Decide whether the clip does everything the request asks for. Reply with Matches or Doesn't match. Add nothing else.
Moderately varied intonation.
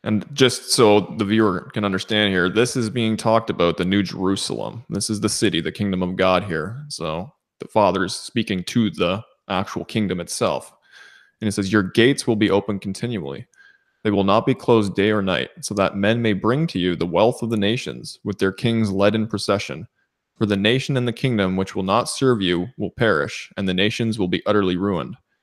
Matches